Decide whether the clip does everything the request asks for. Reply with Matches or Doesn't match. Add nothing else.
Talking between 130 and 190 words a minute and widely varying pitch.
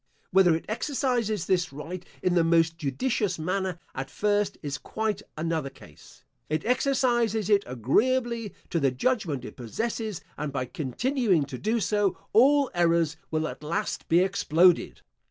Matches